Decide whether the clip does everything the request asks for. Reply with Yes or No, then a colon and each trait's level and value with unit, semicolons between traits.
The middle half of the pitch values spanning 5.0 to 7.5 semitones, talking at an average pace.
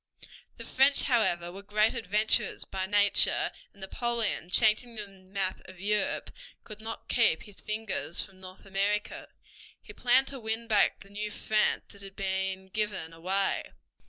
No: narrow, 2.4 semitones; average, 155 wpm